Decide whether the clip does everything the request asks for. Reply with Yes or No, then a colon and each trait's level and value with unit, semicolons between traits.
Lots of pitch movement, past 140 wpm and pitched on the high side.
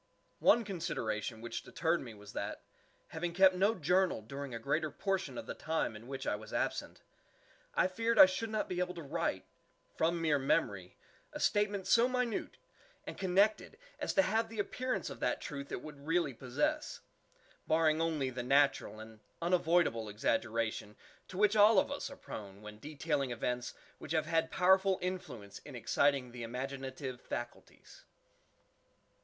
No: wide, 7.5 semitones; average, 160 wpm; medium, 155 Hz